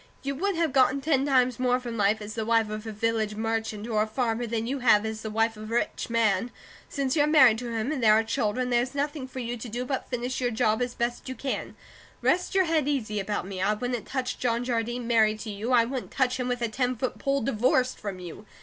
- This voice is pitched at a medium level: No, high, 240 Hz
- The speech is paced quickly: Yes, fast, 250 wpm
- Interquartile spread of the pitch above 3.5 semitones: No, average, 2.8 semitones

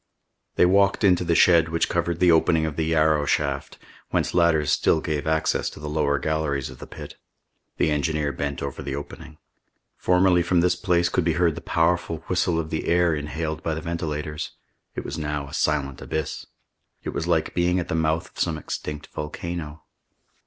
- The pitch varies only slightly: Yes, narrow, 2.2 semitones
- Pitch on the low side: Yes, very low, 80 Hz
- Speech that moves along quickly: No, average, 190 wpm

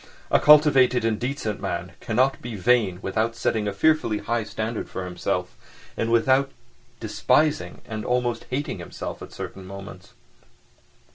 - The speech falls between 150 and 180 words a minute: No, average, 140 wpm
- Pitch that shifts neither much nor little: Yes, average, 3.8 semitones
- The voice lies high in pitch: No, low, 115 Hz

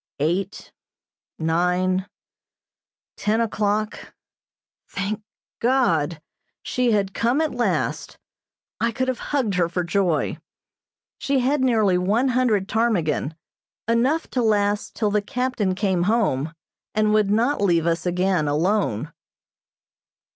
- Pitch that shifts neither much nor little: Yes, average, 4.6 semitones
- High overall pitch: Yes, high, 205 Hz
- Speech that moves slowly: Yes, slow, 115 wpm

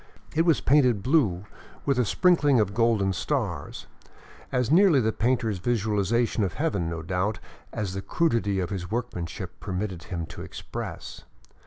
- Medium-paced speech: Yes, average, 150 wpm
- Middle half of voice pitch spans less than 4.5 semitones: No, average, 5.1 semitones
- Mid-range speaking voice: No, low, 110 Hz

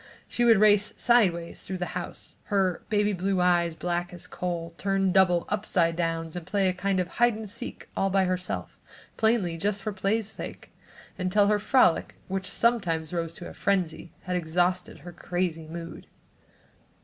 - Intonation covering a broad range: No, average, 2.7 semitones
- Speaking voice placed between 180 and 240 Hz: Yes, medium, 185 Hz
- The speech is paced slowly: No, average, 175 wpm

